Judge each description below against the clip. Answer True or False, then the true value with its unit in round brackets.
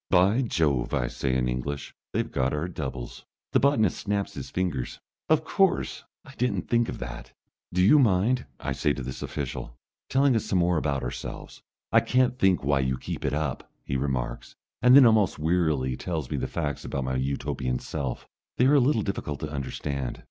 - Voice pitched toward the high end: False (80 Hz)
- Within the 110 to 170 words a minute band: False (190 wpm)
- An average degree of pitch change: False (8.9 semitones)